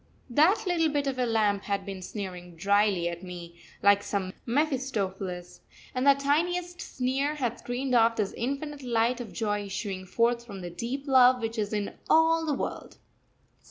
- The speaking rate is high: No, average, 170 wpm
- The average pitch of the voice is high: Yes, high, 235 Hz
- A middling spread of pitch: No, wide, 5.7 semitones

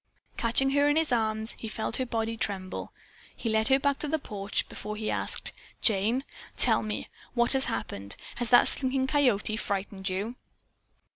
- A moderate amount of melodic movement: Yes, average, 3.9 semitones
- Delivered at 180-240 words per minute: No, average, 170 wpm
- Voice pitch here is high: Yes, high, 225 Hz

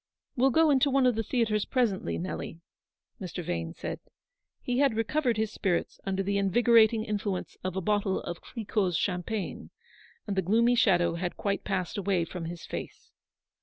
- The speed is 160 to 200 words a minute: Yes, average, 175 wpm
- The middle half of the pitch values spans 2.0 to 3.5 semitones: No, average, 4.4 semitones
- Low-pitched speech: No, high, 200 Hz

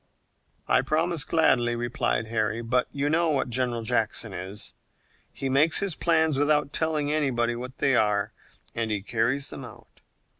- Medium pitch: No, low, 130 Hz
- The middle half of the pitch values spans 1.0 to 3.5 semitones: No, average, 4.6 semitones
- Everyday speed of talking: Yes, average, 155 wpm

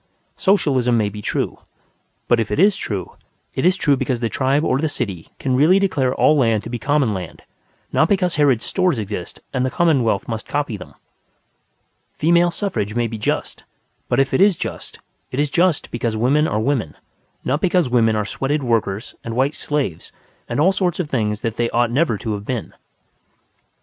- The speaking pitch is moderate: No, low, 130 Hz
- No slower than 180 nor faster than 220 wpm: Yes, average, 190 wpm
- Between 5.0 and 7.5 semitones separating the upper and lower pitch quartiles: Yes, average, 5.3 semitones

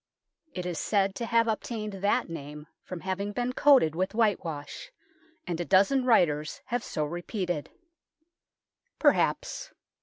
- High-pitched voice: Yes, high, 195 Hz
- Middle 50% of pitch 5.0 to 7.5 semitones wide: Yes, wide, 5.4 semitones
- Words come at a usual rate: No, slow, 130 wpm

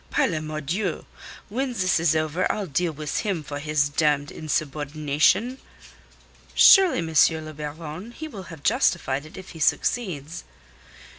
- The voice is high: No, medium, 155 Hz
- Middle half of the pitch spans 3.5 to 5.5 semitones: Yes, average, 4.2 semitones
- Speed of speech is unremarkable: Yes, average, 145 wpm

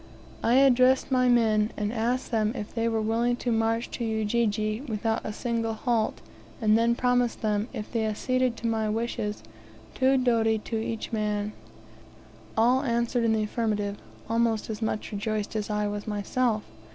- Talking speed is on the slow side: No, average, 165 wpm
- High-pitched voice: Yes, high, 225 Hz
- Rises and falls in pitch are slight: Yes, narrow, 1.8 semitones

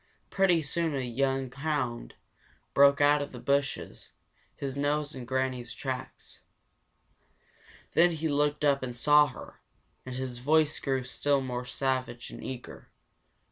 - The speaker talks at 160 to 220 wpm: No, average, 140 wpm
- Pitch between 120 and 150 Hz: Yes, medium, 140 Hz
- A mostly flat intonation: Yes, narrow, 2.3 semitones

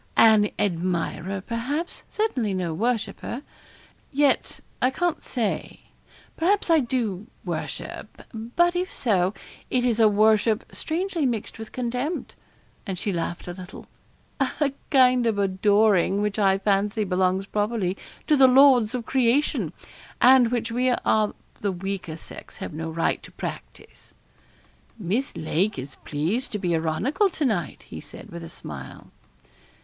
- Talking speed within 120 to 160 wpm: Yes, average, 140 wpm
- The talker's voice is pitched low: No, high, 220 Hz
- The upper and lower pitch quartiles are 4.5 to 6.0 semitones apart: Yes, average, 5.1 semitones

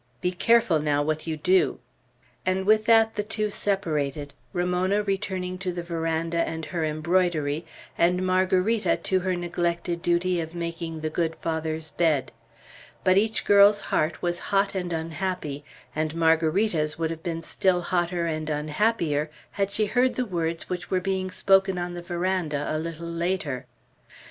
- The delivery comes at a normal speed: Yes, average, 160 wpm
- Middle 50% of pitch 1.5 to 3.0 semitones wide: Yes, average, 2.7 semitones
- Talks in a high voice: No, medium, 175 Hz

